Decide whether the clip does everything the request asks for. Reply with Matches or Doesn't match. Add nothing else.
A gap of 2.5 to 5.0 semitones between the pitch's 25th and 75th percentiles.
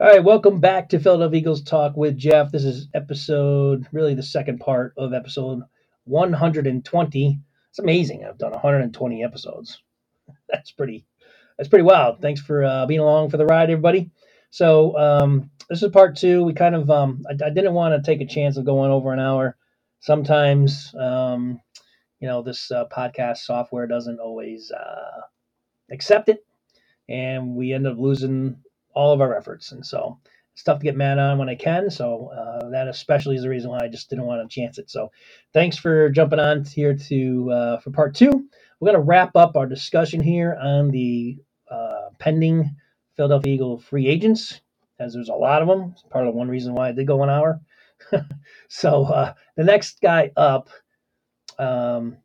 Matches